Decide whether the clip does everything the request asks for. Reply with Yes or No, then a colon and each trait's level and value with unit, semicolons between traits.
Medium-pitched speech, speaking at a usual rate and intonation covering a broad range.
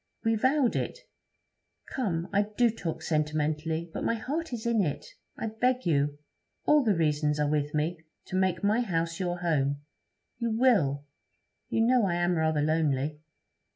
Yes: medium, 175 Hz; average, 160 wpm; wide, 6.8 semitones